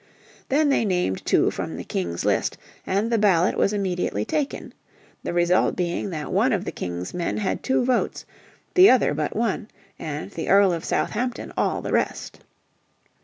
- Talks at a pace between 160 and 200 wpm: Yes, average, 170 wpm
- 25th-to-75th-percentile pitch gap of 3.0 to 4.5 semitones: No, wide, 5.6 semitones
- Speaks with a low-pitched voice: No, high, 190 Hz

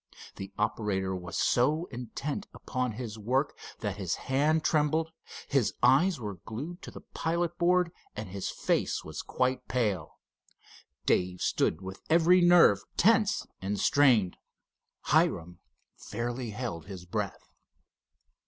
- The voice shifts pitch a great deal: Yes, wide, 7.9 semitones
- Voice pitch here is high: No, low, 125 Hz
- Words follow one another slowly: Yes, slow, 125 wpm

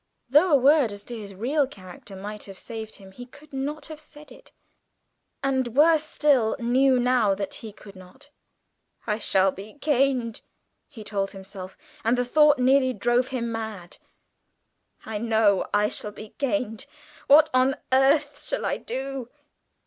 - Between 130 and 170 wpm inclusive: Yes, average, 160 wpm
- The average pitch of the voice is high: Yes, high, 245 Hz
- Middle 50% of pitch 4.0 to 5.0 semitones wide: Yes, average, 4.7 semitones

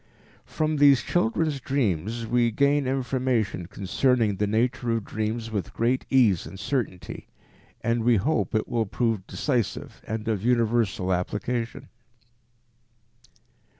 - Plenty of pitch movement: No, average, 3.4 semitones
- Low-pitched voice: Yes, low, 115 Hz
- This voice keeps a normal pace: No, slow, 120 wpm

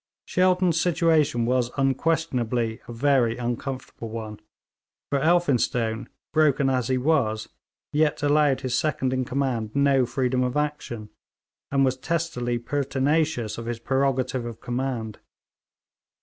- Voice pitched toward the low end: Yes, low, 130 Hz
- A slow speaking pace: Yes, slow, 120 wpm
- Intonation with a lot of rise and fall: No, average, 3.5 semitones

